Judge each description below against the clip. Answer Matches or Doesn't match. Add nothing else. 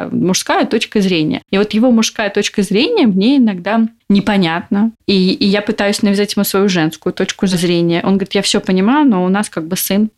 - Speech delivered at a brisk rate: Matches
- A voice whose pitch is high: Matches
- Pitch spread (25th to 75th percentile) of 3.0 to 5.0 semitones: Doesn't match